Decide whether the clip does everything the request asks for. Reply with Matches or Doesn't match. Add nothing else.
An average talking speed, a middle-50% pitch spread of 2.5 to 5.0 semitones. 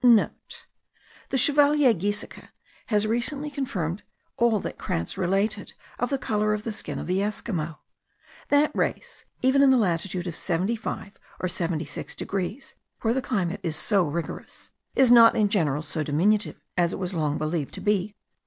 Doesn't match